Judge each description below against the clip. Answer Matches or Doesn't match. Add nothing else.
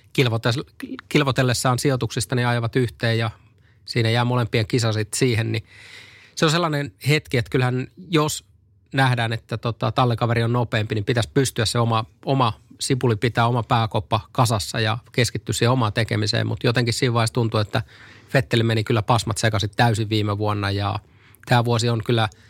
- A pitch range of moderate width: Doesn't match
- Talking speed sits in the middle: Doesn't match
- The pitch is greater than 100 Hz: Matches